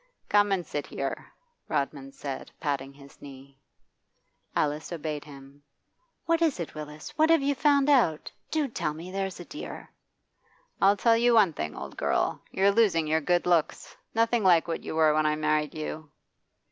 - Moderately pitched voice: Yes, medium, 160 Hz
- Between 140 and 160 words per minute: No, average, 170 wpm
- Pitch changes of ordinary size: No, wide, 5.8 semitones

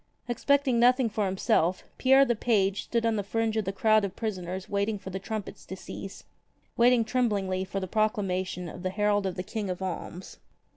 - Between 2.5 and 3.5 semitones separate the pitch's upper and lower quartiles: Yes, average, 3.2 semitones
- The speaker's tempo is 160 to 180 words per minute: No, average, 195 wpm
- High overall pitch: Yes, high, 205 Hz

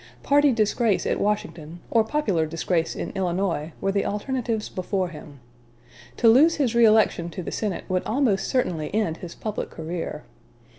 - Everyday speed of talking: Yes, average, 155 wpm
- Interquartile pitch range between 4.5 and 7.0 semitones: Yes, average, 5.0 semitones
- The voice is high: Yes, high, 200 Hz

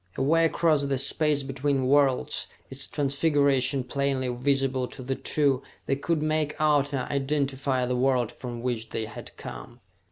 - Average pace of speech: Yes, average, 155 wpm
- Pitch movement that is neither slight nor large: No, narrow, 2.1 semitones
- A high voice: No, low, 135 Hz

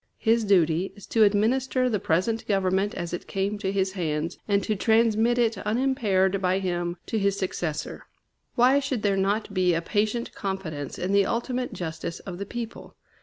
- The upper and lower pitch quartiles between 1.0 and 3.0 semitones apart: No, average, 3.4 semitones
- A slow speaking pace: No, average, 175 wpm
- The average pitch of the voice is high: Yes, high, 200 Hz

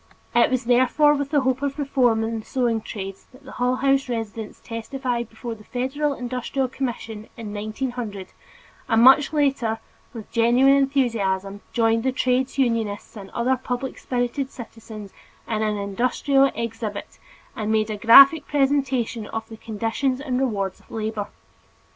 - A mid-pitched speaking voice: No, high, 240 Hz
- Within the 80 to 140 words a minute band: No, average, 155 wpm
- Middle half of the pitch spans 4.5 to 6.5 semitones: No, average, 3.3 semitones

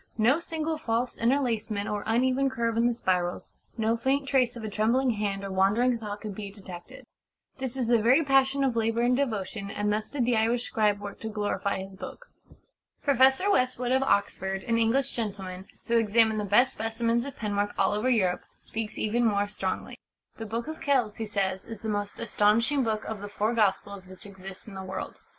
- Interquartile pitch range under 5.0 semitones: Yes, average, 3.3 semitones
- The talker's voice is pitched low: No, high, 225 Hz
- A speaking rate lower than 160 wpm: No, average, 200 wpm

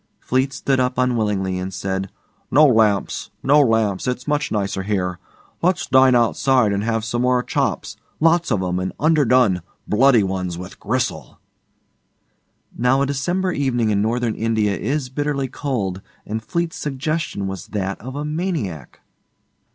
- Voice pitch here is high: No, low, 120 Hz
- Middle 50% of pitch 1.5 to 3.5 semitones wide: No, wide, 5.5 semitones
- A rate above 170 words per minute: No, average, 150 wpm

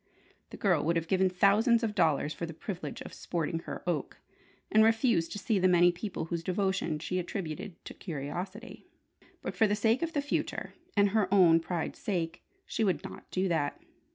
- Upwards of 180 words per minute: Yes, average, 190 wpm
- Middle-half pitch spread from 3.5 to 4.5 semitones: Yes, average, 3.9 semitones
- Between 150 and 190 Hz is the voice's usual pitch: Yes, medium, 185 Hz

